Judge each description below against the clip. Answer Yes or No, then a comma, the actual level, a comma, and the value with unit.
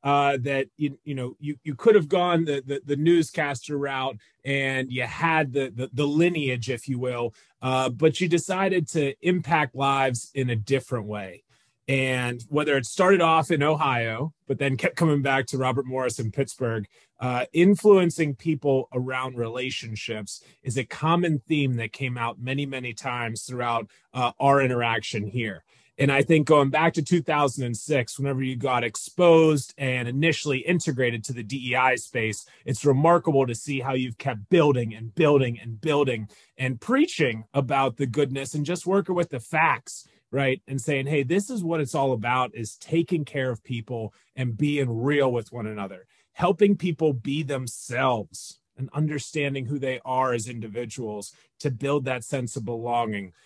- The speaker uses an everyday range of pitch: Yes, average, 3.4 semitones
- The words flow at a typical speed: Yes, average, 170 wpm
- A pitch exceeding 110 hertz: Yes, low, 135 Hz